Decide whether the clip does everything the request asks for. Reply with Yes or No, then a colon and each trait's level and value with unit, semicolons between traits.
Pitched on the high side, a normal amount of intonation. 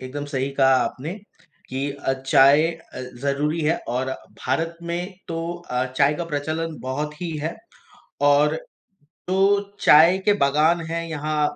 No: medium, 150 Hz; average, 3.1 semitones